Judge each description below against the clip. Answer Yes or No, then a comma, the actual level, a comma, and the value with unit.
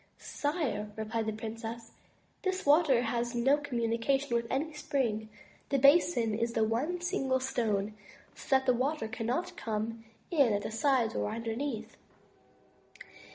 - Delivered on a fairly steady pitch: No, average, 3.9 semitones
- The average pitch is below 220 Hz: No, high, 235 Hz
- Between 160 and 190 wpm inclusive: No, average, 140 wpm